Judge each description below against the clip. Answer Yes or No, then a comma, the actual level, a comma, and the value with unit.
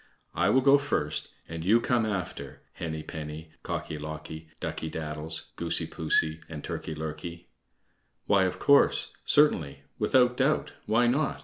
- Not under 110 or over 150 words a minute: Yes, average, 140 wpm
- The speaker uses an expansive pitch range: Yes, wide, 7.6 semitones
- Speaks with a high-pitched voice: No, very low, 80 Hz